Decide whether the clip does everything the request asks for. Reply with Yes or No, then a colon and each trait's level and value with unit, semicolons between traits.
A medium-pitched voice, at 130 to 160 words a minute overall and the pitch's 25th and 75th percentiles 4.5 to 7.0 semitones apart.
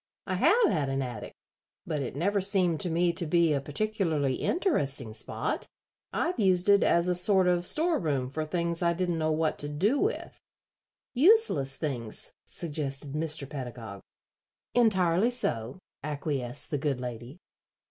Yes: medium, 160 Hz; average, 155 wpm; average, 5.2 semitones